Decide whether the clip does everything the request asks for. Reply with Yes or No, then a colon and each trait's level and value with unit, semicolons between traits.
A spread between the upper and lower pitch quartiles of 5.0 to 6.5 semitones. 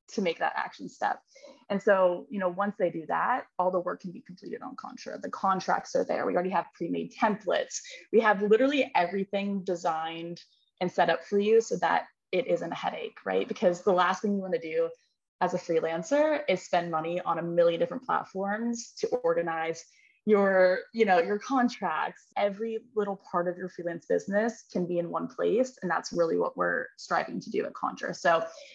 Yes: wide, 5.4 semitones